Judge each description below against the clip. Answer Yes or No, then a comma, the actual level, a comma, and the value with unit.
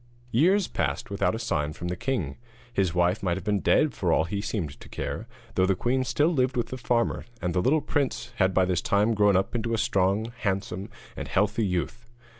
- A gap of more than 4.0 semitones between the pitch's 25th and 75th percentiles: Yes, average, 4.6 semitones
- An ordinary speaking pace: No, fast, 220 wpm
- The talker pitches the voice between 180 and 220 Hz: No, low, 105 Hz